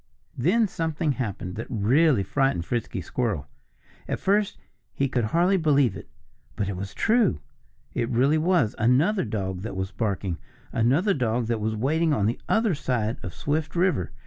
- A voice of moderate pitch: No, low, 125 Hz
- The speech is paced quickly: No, average, 165 wpm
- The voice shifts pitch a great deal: Yes, wide, 7.2 semitones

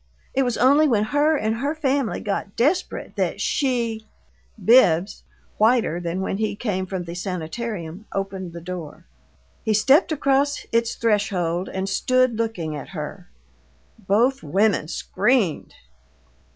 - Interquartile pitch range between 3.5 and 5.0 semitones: No, wide, 5.6 semitones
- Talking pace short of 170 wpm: Yes, average, 140 wpm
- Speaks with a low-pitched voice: No, high, 215 Hz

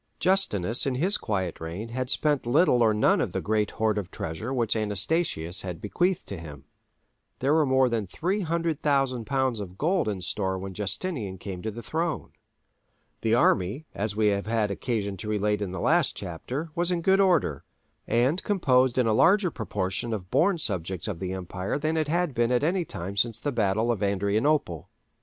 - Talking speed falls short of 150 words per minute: No, average, 190 wpm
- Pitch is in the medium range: No, low, 115 Hz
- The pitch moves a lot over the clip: Yes, wide, 7.2 semitones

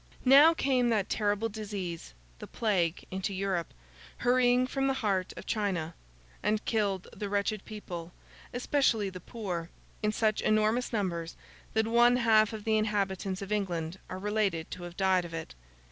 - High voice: Yes, high, 205 Hz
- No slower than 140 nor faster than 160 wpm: Yes, average, 150 wpm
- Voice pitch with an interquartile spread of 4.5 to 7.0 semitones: No, average, 3.3 semitones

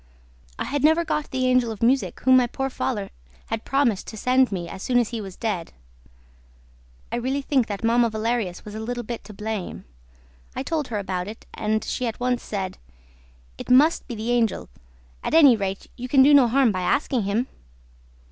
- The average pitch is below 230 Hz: No, high, 235 Hz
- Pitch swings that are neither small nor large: Yes, average, 3.4 semitones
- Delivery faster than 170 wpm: Yes, average, 200 wpm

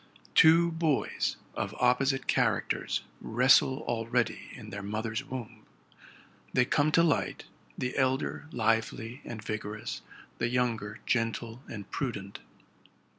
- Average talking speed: No, slow, 115 wpm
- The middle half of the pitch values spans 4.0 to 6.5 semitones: No, average, 3.1 semitones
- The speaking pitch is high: No, low, 120 Hz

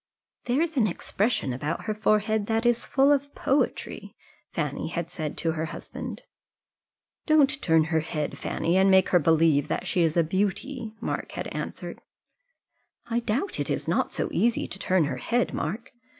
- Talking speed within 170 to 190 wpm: Yes, average, 180 wpm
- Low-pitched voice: No, high, 200 Hz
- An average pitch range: No, wide, 6.7 semitones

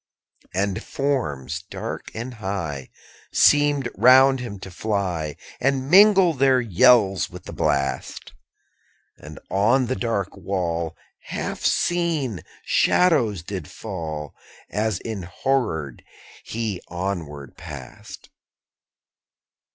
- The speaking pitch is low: Yes, low, 100 Hz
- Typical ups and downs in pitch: No, wide, 7.5 semitones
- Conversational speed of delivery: No, slow, 105 wpm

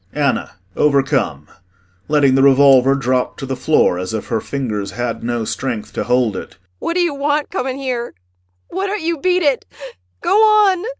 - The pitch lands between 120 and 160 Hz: Yes, medium, 140 Hz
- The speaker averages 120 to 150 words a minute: No, average, 175 wpm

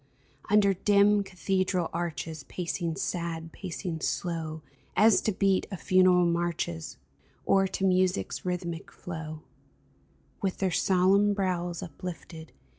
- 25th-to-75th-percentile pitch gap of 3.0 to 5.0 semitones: No, narrow, 2.6 semitones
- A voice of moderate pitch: Yes, medium, 180 Hz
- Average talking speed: No, slow, 115 wpm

